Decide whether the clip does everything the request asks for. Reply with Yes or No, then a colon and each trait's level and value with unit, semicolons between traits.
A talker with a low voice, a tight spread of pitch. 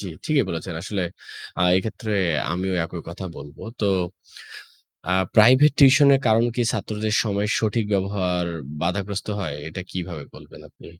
No: low, 100 Hz; average, 3.6 semitones